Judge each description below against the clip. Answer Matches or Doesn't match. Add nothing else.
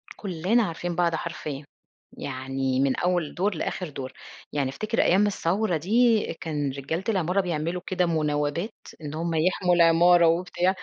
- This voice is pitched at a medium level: Matches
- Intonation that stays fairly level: Doesn't match